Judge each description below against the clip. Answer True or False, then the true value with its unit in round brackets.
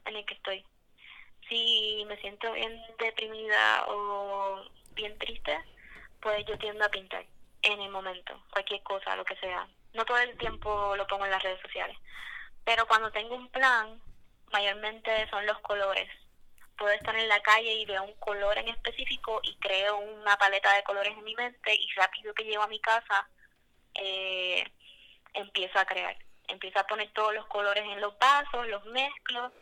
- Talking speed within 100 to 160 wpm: False (175 wpm)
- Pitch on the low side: False (210 Hz)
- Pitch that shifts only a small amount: True (2.0 semitones)